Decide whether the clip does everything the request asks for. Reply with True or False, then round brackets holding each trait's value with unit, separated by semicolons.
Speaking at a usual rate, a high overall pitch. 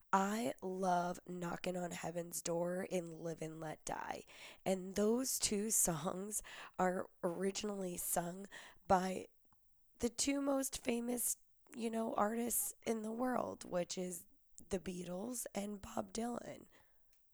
False (125 wpm; 195 Hz)